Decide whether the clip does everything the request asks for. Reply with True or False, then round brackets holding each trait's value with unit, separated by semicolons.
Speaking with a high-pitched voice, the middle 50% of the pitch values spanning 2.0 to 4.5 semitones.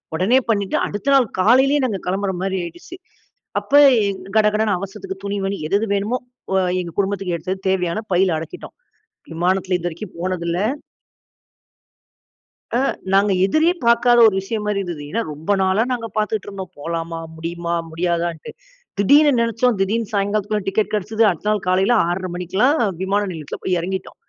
True (195 Hz; 3.2 semitones)